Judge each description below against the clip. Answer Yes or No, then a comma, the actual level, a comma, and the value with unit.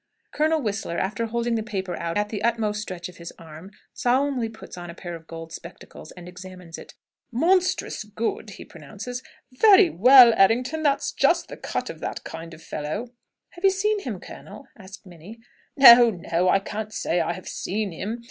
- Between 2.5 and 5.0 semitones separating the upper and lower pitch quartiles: No, wide, 5.6 semitones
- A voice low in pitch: No, high, 210 Hz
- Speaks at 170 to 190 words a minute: Yes, average, 185 wpm